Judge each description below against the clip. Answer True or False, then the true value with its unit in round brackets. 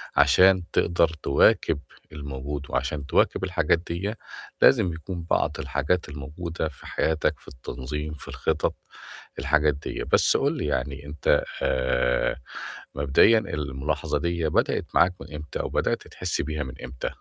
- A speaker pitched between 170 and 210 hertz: False (75 Hz)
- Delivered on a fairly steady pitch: False (3.3 semitones)